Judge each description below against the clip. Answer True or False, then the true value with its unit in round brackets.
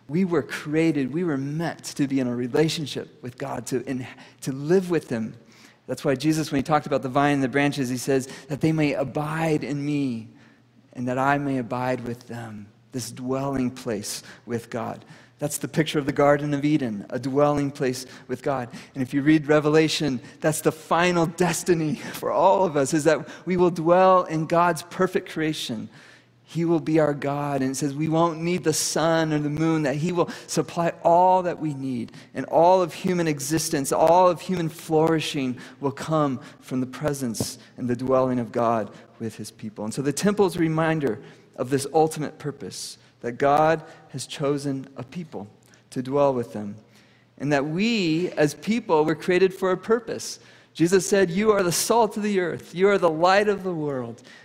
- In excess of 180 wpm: True (195 wpm)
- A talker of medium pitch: True (150 Hz)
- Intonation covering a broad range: False (3.9 semitones)